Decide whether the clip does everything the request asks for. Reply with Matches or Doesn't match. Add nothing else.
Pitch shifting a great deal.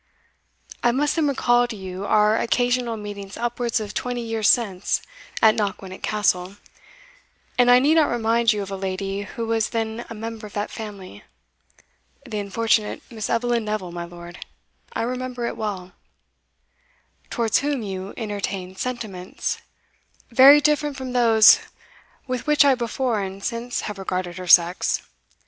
Doesn't match